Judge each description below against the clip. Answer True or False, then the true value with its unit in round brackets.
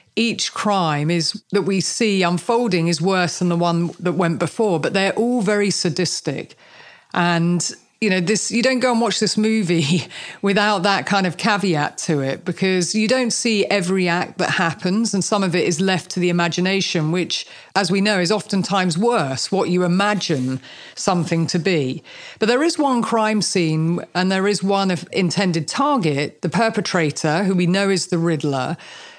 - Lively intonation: False (3.3 semitones)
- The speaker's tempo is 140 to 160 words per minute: False (185 wpm)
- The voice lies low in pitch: False (185 Hz)